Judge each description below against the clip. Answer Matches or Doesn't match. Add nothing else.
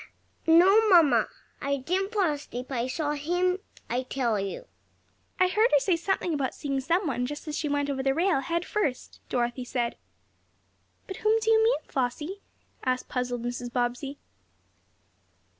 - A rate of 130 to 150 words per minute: Doesn't match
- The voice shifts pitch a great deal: Matches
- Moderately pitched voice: Doesn't match